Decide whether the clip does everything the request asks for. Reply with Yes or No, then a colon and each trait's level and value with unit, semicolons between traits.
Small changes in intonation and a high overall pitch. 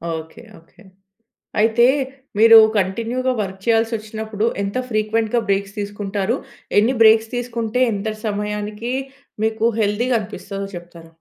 Yes: narrow, 2.1 semitones; high, 215 Hz